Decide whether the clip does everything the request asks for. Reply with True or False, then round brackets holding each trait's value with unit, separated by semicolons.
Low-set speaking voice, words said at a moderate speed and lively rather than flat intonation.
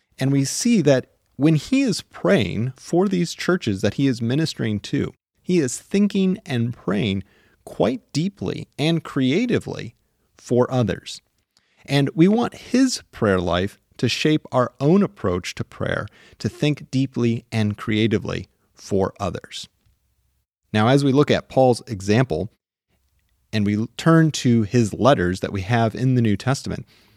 True (125 Hz; 150 wpm; 6.3 semitones)